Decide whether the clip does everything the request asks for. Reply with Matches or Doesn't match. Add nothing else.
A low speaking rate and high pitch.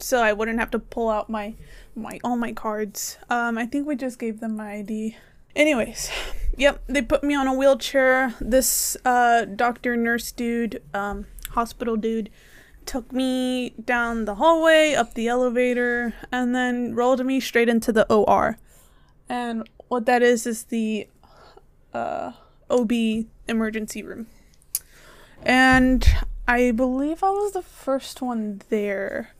Doesn't match